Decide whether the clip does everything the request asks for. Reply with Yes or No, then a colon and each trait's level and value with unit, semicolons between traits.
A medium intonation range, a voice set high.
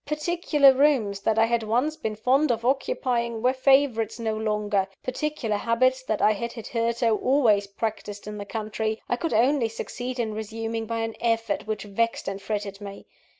Yes: average, 3.1 semitones; high, 230 Hz